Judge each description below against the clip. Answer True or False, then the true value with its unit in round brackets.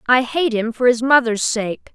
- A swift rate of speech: True (215 wpm)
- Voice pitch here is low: False (240 Hz)